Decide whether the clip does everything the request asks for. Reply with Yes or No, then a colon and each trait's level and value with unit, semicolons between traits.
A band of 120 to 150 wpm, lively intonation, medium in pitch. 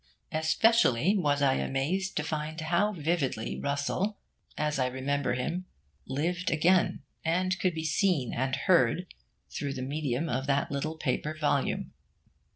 No: average, 140 wpm; average, 4.4 semitones; medium, 150 Hz